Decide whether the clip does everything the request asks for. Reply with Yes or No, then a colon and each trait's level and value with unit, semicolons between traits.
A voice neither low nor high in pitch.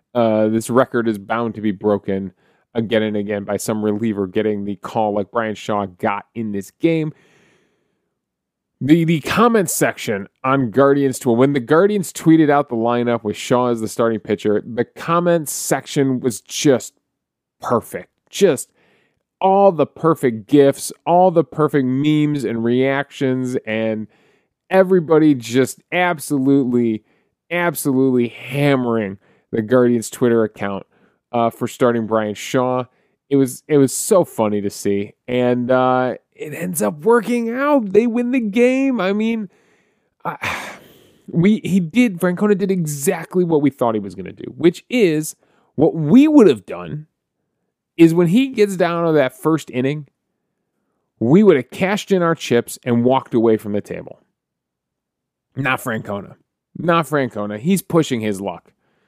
No: low, 130 Hz